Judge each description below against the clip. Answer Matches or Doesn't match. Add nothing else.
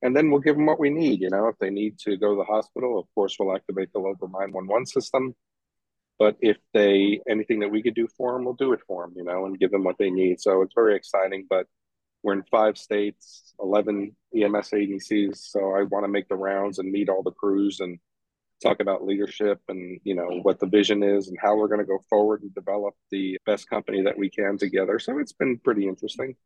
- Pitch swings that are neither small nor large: Doesn't match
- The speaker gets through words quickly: Matches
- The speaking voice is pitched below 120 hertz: Matches